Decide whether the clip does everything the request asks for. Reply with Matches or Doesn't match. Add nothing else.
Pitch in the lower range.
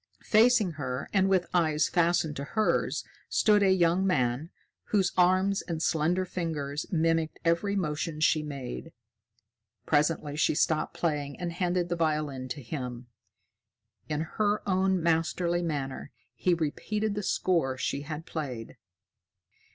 Doesn't match